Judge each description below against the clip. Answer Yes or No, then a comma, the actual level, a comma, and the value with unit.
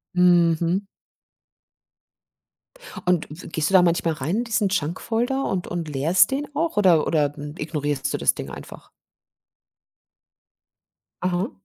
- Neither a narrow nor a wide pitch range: Yes, average, 4.2 semitones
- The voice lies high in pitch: No, medium, 175 Hz